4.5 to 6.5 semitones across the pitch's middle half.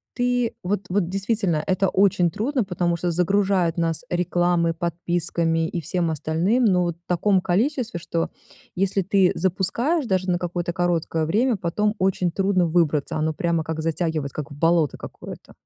No: average, 2.9 semitones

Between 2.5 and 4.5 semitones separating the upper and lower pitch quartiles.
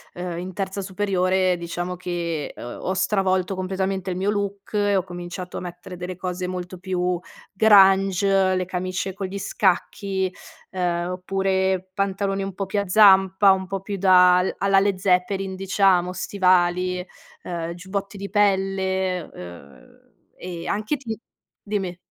No: narrow, 1.3 semitones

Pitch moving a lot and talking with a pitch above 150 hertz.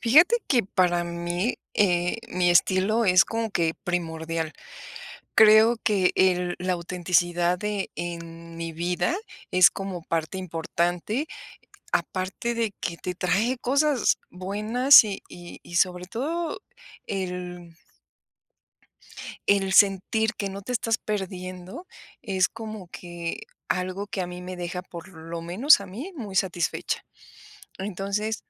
No: average, 3.4 semitones; medium, 185 Hz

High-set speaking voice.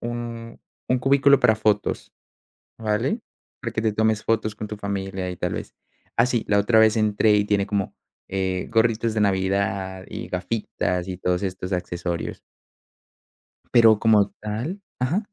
No: low, 105 Hz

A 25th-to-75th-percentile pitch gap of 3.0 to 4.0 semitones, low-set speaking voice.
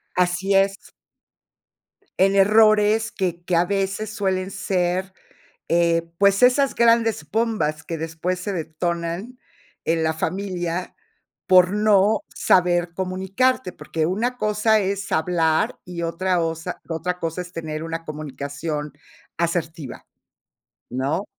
No: average, 3.3 semitones; medium, 180 Hz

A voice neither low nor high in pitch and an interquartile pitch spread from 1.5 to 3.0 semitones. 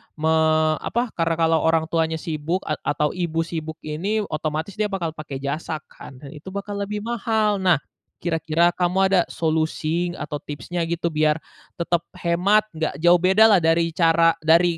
Yes: medium, 165 Hz; narrow, 2.6 semitones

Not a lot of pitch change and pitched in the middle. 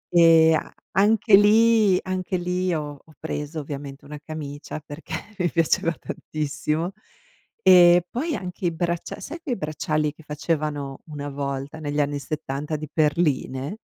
No: average, 3.5 semitones; medium, 155 Hz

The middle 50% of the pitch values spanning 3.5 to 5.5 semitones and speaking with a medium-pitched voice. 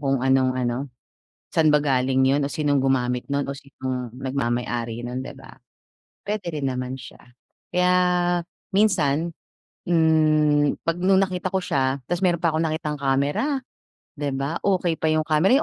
Yes: average, 3.9 semitones; medium, 145 Hz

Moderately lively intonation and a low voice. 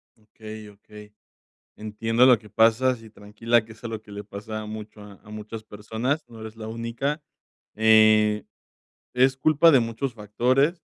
No: narrow, 2.1 semitones; low, 110 Hz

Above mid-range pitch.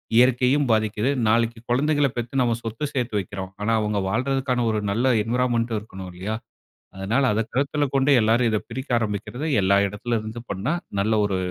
No: low, 115 Hz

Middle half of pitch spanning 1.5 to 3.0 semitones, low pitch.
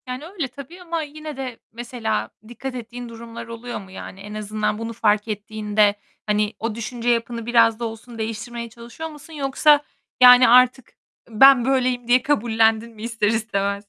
No: narrow, 2.6 semitones; high, 235 Hz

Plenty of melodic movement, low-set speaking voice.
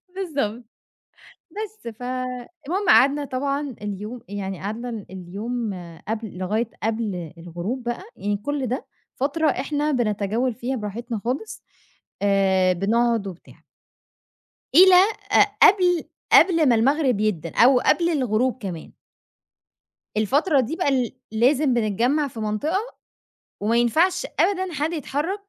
No: wide, 5.7 semitones; high, 245 Hz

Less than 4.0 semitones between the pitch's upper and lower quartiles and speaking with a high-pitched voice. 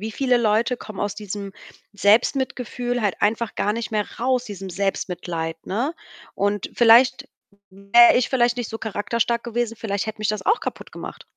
Yes: average, 2.9 semitones; high, 220 Hz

